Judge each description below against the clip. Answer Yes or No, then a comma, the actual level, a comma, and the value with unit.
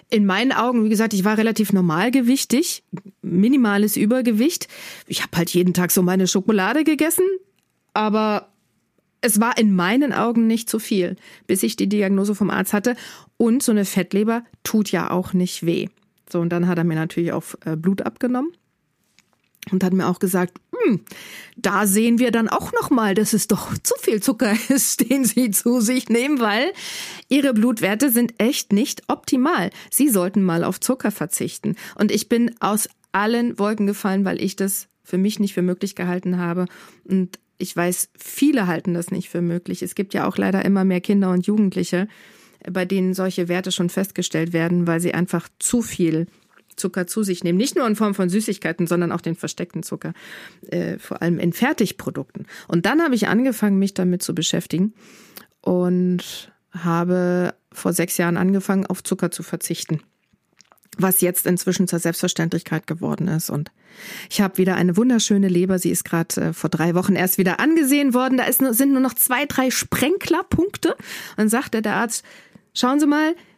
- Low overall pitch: No, high, 195 Hz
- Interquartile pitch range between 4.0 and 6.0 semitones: Yes, average, 4.3 semitones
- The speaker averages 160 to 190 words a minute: Yes, average, 180 wpm